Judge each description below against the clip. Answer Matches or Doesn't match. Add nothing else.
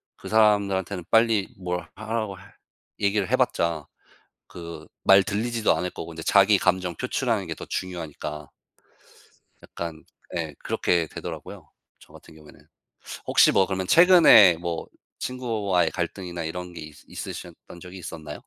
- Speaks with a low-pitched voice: Matches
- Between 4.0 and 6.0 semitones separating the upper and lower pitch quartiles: Doesn't match